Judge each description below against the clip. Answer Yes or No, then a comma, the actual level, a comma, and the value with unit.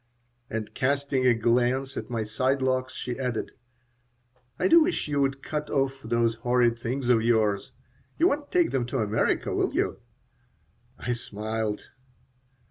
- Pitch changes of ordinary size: Yes, average, 3.0 semitones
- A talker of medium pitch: No, low, 125 Hz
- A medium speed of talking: Yes, average, 150 wpm